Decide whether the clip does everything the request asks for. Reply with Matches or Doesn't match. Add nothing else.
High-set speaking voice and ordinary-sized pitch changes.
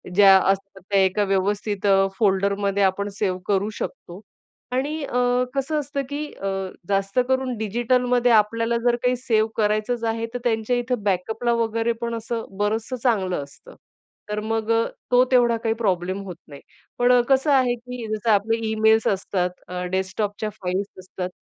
Matches